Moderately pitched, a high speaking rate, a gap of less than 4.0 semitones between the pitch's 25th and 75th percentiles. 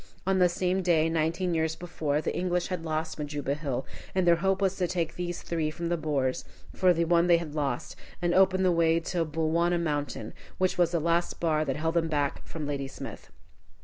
Yes: medium, 165 Hz; fast, 210 wpm; narrow, 2.4 semitones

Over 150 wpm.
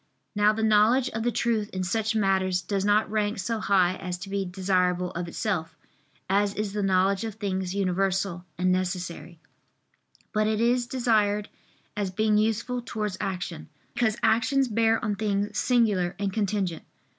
Yes: average, 160 wpm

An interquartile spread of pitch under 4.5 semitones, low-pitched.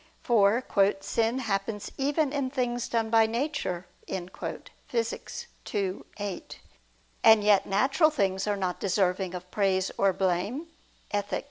No: average, 4.0 semitones; high, 205 Hz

